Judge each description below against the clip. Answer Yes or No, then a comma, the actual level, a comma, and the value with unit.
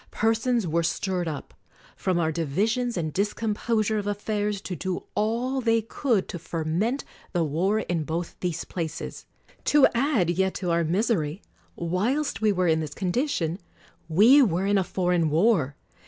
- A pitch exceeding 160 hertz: Yes, high, 190 Hz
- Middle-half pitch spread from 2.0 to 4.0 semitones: No, average, 4.9 semitones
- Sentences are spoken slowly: No, average, 160 wpm